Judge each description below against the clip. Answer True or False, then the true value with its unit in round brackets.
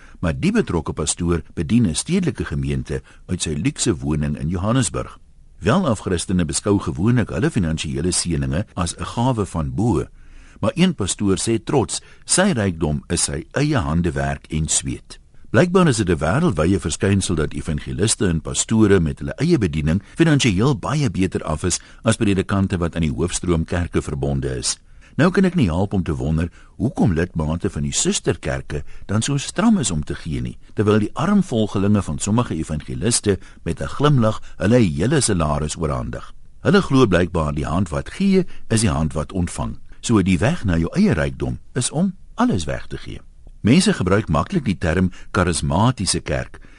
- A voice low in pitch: True (90 Hz)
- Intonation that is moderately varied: False (6.4 semitones)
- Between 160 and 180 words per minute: True (170 wpm)